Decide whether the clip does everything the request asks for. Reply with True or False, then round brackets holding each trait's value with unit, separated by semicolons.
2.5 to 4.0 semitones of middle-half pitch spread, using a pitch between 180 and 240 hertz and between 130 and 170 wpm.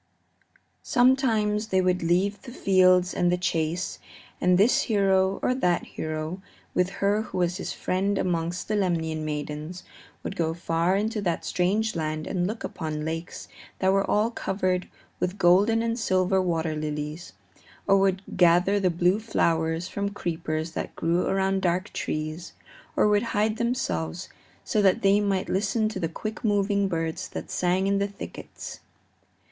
True (3.3 semitones; 185 Hz; 160 wpm)